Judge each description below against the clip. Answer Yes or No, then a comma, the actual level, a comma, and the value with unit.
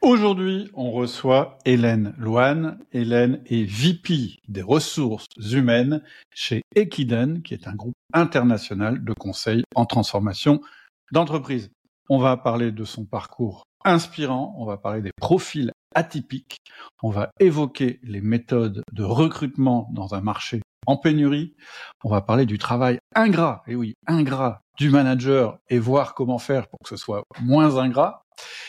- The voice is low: Yes, low, 125 Hz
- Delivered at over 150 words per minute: No, slow, 145 wpm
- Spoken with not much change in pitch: No, average, 4.5 semitones